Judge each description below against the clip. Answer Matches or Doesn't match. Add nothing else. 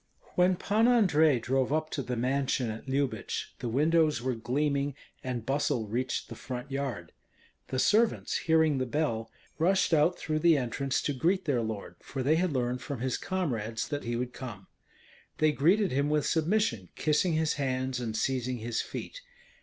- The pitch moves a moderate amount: Matches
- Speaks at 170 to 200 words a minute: Matches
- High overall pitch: Doesn't match